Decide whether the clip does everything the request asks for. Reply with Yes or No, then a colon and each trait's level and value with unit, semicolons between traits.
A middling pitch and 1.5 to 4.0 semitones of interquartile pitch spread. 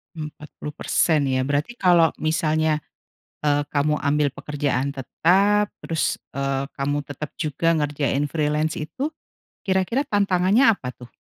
Yes: medium, 150 Hz; average, 3.6 semitones